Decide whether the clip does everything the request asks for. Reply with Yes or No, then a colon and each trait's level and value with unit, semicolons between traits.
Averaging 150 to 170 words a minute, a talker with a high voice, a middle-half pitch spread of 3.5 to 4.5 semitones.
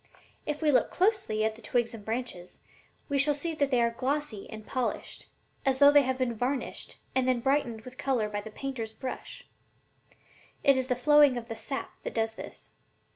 No: average, 195 wpm; very high, 255 Hz; average, 3.8 semitones